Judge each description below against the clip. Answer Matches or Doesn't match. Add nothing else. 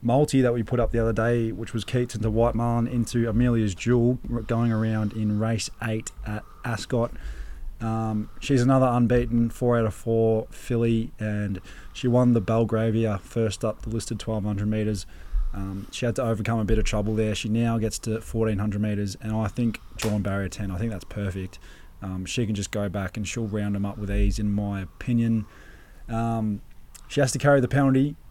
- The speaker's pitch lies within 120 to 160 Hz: Doesn't match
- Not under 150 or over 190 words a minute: Doesn't match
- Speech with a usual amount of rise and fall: Doesn't match